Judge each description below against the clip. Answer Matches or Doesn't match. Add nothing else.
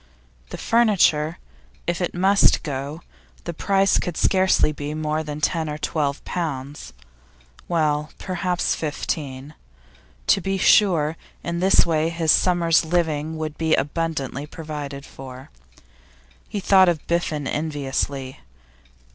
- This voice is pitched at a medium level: Matches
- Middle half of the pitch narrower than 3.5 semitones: Matches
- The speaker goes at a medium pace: Doesn't match